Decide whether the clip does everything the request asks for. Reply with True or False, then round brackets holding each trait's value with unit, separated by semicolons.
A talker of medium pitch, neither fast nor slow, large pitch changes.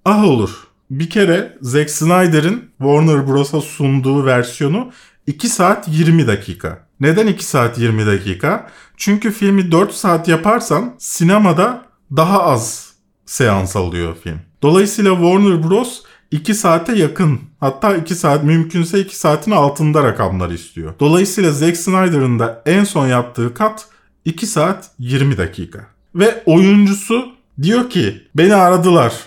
True (165 Hz; 130 wpm; 6.4 semitones)